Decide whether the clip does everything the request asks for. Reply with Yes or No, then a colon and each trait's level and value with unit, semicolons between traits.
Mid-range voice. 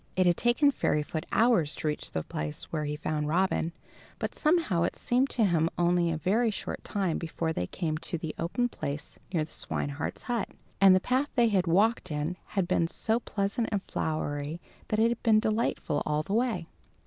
Yes: medium, 180 Hz